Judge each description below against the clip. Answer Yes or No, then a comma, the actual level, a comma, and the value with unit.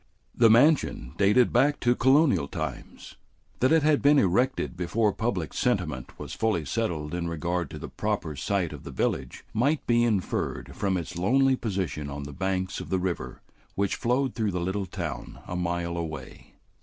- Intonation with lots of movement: Yes, wide, 6.0 semitones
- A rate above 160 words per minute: Yes, average, 175 wpm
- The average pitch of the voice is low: Yes, very low, 95 Hz